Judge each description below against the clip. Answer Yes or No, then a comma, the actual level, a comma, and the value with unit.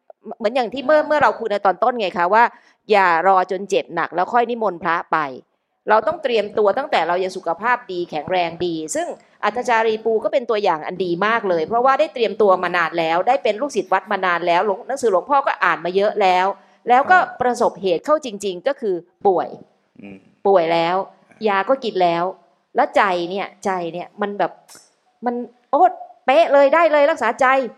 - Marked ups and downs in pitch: Yes, wide, 5.7 semitones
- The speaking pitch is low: No, high, 205 Hz